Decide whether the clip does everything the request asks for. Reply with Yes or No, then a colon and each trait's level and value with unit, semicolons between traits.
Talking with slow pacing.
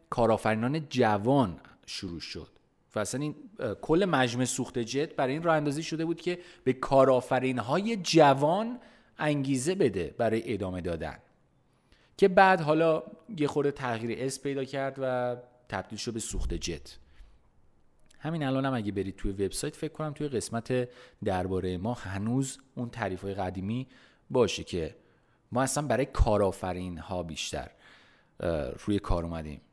No: average, 145 wpm